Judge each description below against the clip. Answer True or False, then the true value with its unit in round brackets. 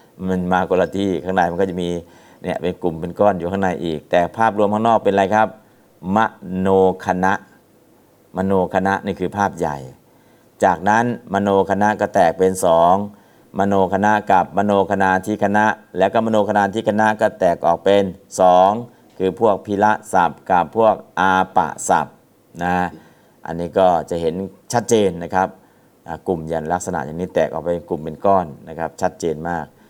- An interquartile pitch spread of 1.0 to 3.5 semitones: True (2.4 semitones)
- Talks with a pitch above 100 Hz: False (95 Hz)